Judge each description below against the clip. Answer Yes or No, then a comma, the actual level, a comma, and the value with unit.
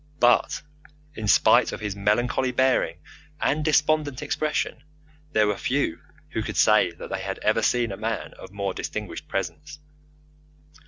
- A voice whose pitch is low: Yes, low, 115 Hz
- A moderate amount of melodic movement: No, wide, 5.8 semitones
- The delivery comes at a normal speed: Yes, average, 150 wpm